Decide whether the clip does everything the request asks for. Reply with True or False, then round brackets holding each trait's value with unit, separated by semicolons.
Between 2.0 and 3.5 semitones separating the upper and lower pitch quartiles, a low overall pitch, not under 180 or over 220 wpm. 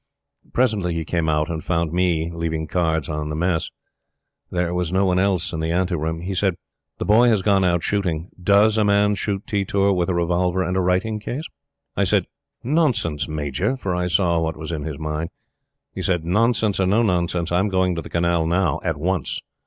True (3.2 semitones; 90 Hz; 200 wpm)